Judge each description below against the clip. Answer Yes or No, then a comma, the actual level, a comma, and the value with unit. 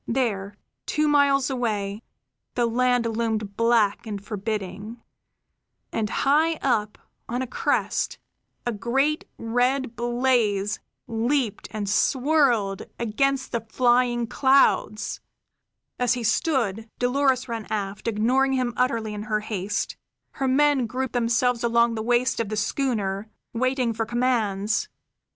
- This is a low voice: No, high, 235 Hz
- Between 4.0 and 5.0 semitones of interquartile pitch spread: No, average, 3.1 semitones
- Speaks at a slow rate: Yes, slow, 125 wpm